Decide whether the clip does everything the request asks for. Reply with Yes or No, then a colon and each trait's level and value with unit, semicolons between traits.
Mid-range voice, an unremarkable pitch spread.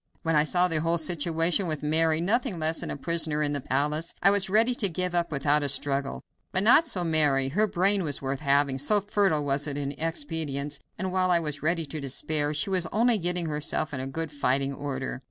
Yes: medium, 160 Hz; average, 3.8 semitones